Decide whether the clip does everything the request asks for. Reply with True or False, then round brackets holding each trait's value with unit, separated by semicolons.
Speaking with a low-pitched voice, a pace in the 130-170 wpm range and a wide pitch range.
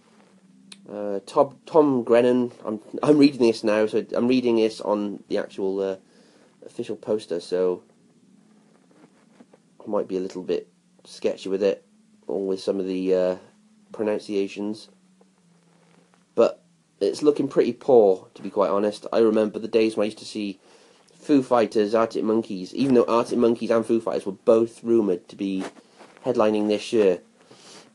True (115 Hz; 155 wpm; 8.7 semitones)